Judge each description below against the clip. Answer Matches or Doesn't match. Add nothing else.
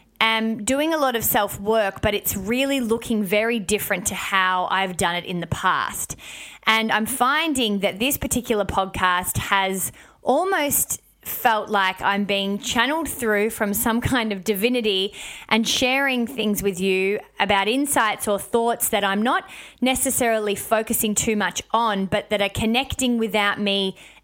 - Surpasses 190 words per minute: Doesn't match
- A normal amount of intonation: Matches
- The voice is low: Doesn't match